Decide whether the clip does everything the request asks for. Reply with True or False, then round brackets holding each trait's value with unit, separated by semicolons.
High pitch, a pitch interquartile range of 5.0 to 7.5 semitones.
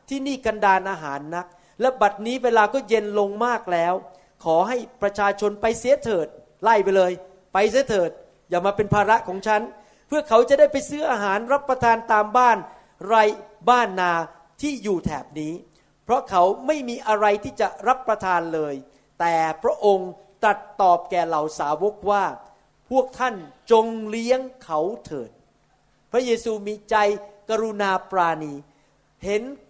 False (210 Hz; 4.6 semitones)